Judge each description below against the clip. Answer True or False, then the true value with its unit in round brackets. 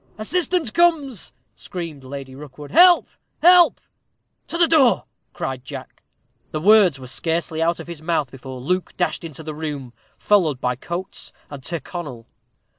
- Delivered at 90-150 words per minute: True (145 wpm)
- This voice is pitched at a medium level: True (165 Hz)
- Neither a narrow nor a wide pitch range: False (7.7 semitones)